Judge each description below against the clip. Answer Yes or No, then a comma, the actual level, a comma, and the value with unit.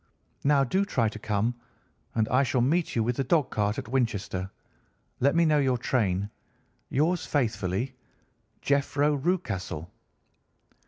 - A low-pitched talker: Yes, low, 125 Hz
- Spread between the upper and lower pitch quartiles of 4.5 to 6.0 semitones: Yes, average, 5.0 semitones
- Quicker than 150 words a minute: No, average, 140 wpm